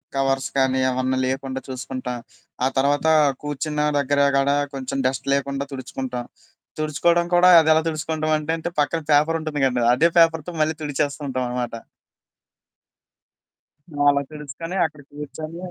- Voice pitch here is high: No, medium, 145 Hz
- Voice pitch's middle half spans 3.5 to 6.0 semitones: No, average, 2.9 semitones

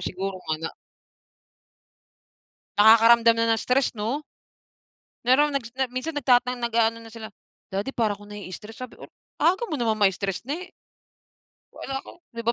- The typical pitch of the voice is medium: No, high, 230 Hz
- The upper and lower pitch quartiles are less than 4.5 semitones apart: Yes, average, 3.4 semitones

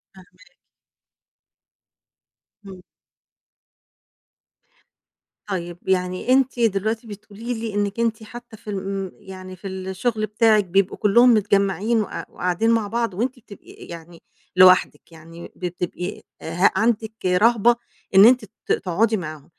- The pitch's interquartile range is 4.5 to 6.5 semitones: No, average, 3.5 semitones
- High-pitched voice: Yes, high, 200 Hz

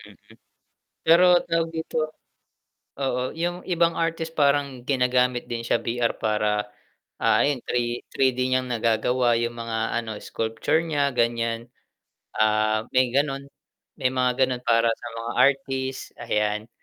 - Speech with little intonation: No, average, 3.2 semitones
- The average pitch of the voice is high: No, low, 125 Hz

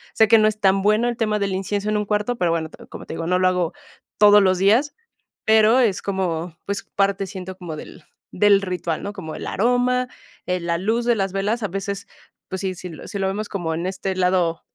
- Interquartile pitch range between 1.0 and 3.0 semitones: Yes, average, 2.7 semitones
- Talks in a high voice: Yes, high, 195 Hz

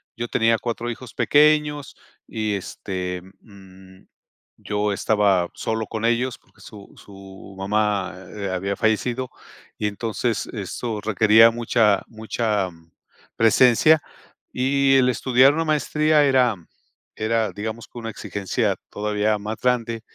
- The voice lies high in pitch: No, low, 110 Hz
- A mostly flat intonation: No, average, 3.2 semitones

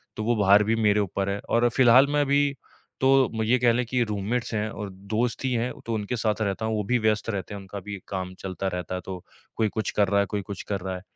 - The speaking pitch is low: Yes, low, 105 Hz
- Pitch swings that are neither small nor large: Yes, average, 3.0 semitones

